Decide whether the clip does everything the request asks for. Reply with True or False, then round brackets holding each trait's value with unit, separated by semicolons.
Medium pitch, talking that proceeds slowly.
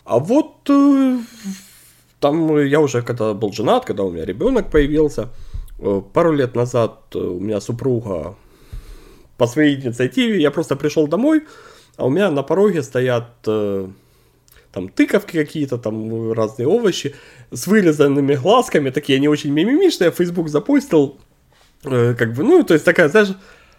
False (145 Hz; 135 wpm)